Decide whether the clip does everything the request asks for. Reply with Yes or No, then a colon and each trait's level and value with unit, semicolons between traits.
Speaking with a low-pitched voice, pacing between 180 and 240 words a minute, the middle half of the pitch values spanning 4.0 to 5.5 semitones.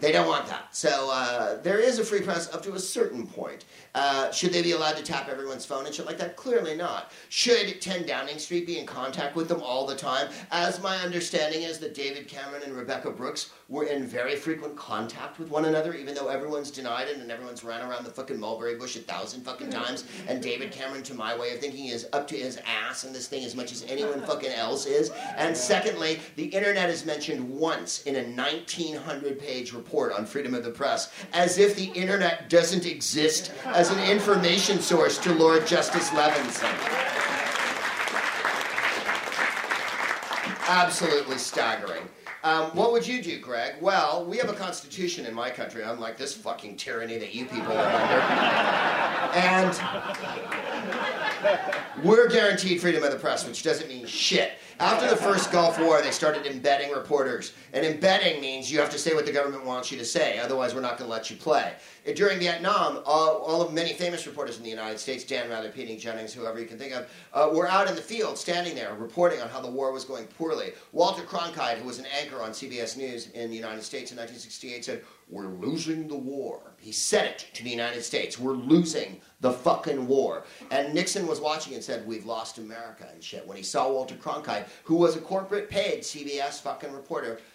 No: medium, 150 Hz; average, 200 wpm; average, 5.2 semitones